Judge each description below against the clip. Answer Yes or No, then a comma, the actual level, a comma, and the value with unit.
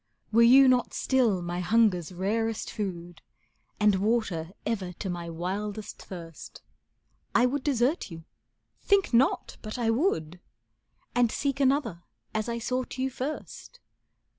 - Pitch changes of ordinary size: No, wide, 5.8 semitones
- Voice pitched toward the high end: Yes, high, 220 Hz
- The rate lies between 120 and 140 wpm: Yes, slow, 135 wpm